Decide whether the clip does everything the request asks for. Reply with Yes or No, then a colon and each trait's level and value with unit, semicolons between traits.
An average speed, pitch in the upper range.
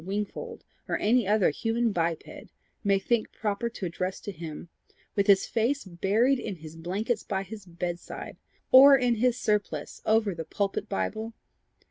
Yes: average, 155 wpm; high, 205 Hz